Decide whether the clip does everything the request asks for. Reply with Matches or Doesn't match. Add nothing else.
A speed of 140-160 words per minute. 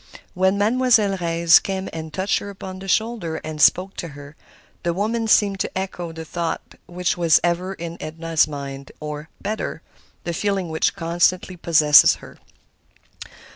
Matches